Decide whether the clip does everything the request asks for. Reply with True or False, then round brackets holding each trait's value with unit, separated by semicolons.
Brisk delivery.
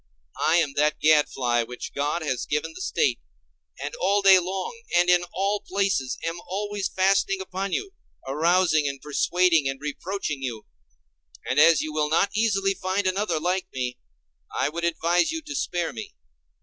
False (165 wpm)